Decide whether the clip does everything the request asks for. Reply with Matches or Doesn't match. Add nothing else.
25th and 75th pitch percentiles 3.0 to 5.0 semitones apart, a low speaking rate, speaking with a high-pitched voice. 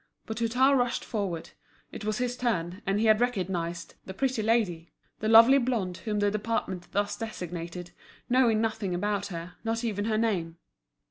Doesn't match